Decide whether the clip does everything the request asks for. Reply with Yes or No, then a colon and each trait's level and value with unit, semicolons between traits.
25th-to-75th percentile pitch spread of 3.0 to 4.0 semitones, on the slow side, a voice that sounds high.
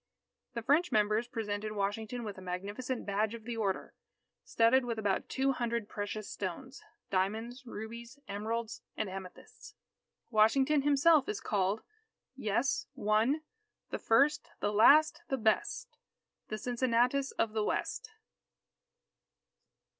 Yes: average, 3.7 semitones; slow, 125 wpm; high, 225 Hz